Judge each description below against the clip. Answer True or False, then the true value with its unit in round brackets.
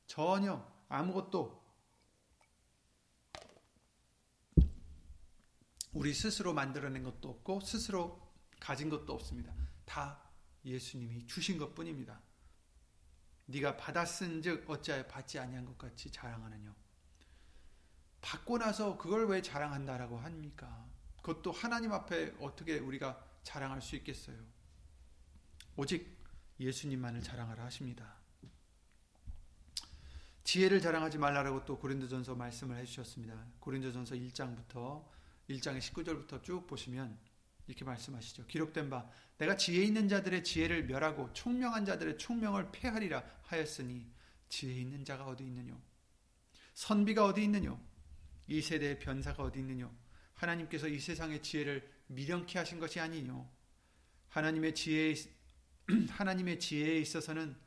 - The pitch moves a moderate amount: False (6.4 semitones)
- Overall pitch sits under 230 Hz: True (135 Hz)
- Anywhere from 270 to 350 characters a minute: True (280 characters per minute)